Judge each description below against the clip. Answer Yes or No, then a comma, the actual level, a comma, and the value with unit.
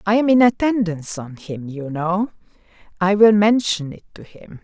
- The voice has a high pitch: Yes, high, 195 Hz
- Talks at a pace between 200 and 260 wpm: No, average, 170 wpm